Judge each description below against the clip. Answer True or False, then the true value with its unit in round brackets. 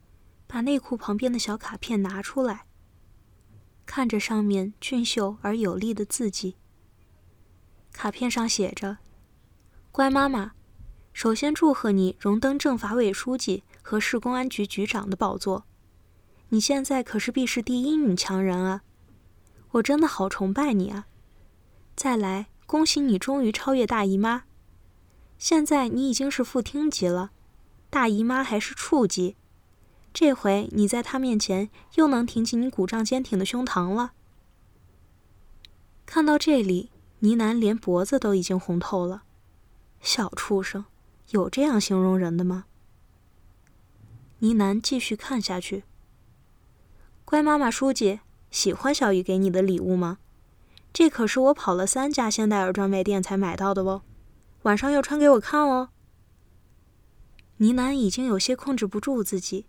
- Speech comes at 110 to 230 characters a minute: True (210 characters per minute)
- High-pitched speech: True (205 Hz)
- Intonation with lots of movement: True (5.7 semitones)